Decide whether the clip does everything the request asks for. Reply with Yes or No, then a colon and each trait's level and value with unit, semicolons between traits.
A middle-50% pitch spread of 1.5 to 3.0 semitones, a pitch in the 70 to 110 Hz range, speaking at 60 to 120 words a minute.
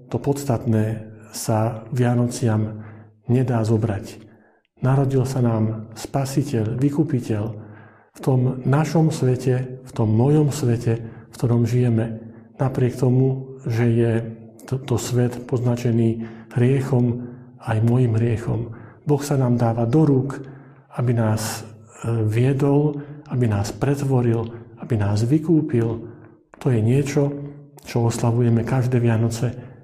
No: average, 2.7 semitones; low, 120 Hz; average, 115 wpm